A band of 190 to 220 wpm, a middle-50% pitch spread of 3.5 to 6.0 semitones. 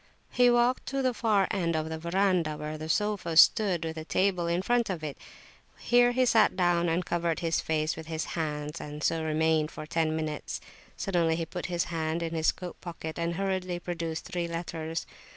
No: average, 200 wpm; average, 2.7 semitones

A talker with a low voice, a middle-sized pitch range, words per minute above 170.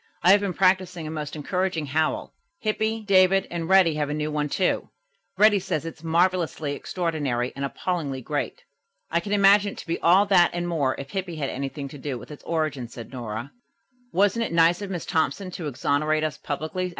No: medium, 165 Hz; average, 4.2 semitones; average, 200 wpm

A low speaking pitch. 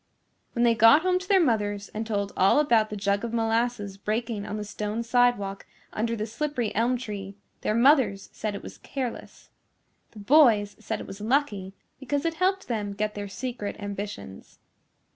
No: high, 220 Hz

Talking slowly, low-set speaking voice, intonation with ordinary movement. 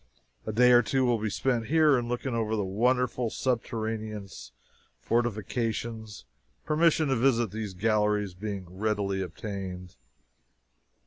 Yes: slow, 125 wpm; low, 110 Hz; average, 3.0 semitones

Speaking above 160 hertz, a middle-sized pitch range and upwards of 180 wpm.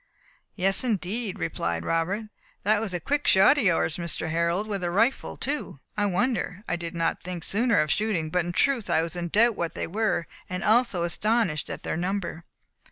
Yes: medium, 185 Hz; average, 4.4 semitones; average, 200 wpm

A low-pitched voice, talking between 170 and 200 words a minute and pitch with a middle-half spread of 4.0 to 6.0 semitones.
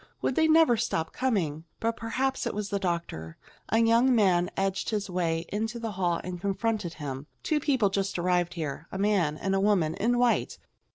No: high, 195 Hz; average, 190 wpm; average, 4.9 semitones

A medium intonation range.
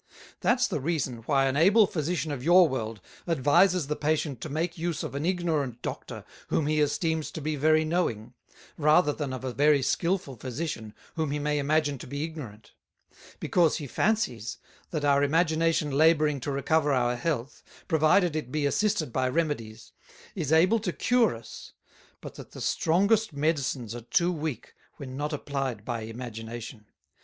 Yes: average, 3.9 semitones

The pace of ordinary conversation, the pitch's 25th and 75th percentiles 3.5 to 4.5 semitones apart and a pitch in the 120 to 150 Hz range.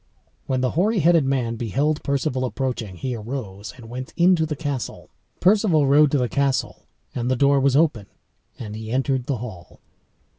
Yes: average, 175 wpm; average, 3.8 semitones; low, 135 Hz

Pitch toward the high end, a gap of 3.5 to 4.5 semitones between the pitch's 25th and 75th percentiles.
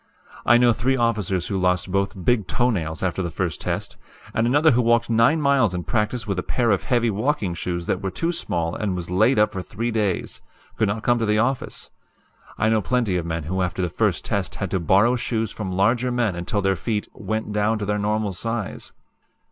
No: low, 105 Hz; average, 4.1 semitones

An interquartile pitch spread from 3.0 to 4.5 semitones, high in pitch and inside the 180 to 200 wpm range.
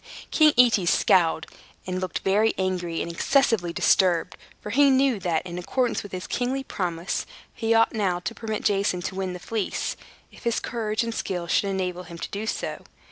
Yes: average, 4.1 semitones; high, 195 Hz; average, 190 wpm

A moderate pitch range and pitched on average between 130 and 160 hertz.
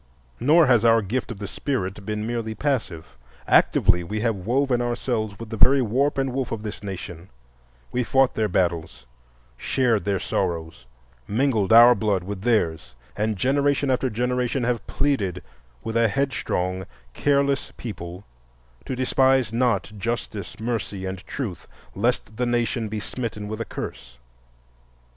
No: average, 4.6 semitones; low, 110 Hz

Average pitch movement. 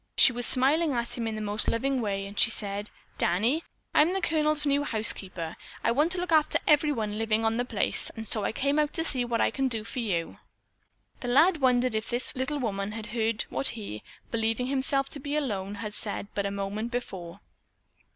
Yes: average, 4.8 semitones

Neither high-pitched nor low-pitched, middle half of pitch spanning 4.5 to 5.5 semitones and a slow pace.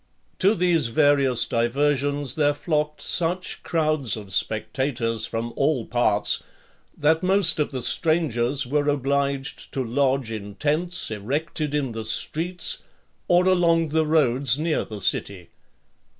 Yes: medium, 145 Hz; average, 4.9 semitones; slow, 130 wpm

